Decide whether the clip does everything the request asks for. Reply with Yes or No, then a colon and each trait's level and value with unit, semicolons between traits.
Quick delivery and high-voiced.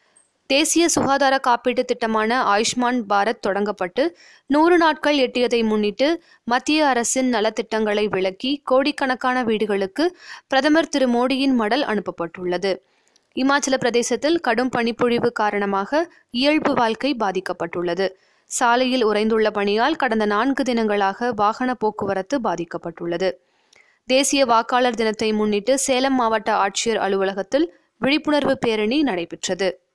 No: average, 100 wpm; high, 240 Hz